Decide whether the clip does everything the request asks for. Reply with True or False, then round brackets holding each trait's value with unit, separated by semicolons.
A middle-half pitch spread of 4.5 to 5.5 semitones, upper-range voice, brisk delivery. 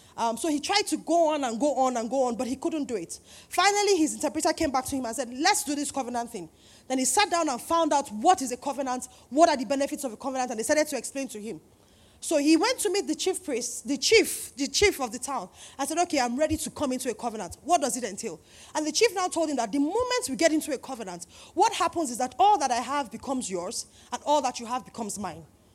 True (4.9 semitones; 280 Hz; 275 wpm)